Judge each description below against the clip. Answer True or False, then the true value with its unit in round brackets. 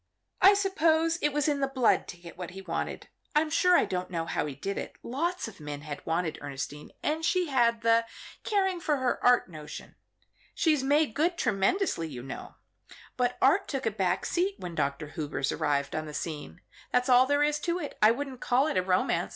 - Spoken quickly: True (210 wpm)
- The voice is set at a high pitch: True (245 Hz)